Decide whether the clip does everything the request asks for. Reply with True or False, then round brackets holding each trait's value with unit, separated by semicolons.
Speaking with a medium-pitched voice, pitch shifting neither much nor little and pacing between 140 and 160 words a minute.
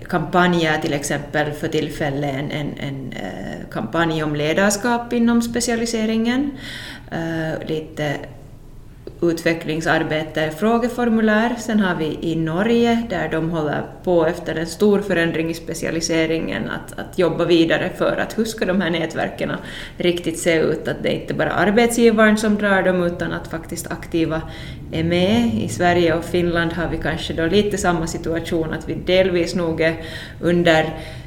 True (165 Hz; 3.0 semitones; 150 wpm)